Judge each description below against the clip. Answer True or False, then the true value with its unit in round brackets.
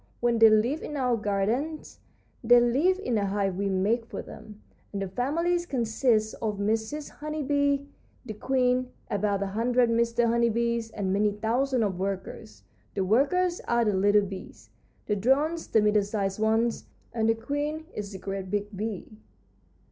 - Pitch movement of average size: True (3.8 semitones)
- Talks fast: False (170 wpm)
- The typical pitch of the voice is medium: False (225 Hz)